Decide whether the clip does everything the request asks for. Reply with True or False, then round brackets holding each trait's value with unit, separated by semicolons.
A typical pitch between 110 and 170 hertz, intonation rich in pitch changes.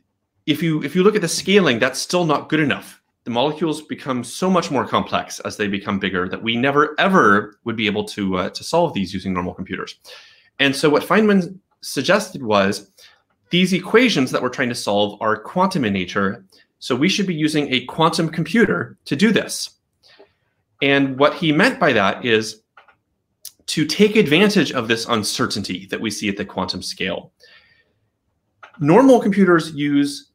True (140 Hz; 8.3 semitones)